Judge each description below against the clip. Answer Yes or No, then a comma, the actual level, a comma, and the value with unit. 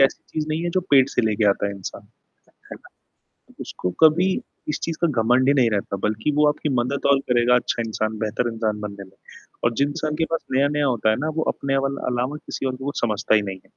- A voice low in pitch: Yes, low, 125 Hz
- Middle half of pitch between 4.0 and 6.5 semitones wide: Yes, average, 5.0 semitones